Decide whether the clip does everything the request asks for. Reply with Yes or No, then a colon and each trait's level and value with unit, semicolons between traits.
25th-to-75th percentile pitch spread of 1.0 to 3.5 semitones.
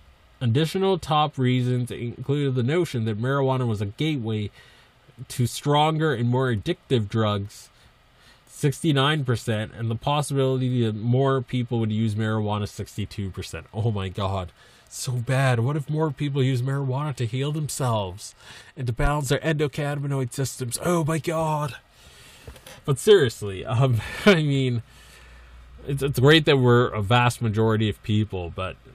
No: average, 4.4 semitones